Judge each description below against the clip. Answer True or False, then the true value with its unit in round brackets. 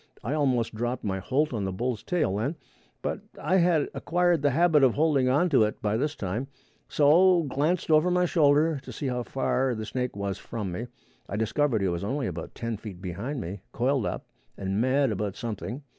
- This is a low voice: True (130 Hz)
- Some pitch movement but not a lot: False (5.8 semitones)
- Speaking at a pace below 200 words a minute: False (205 wpm)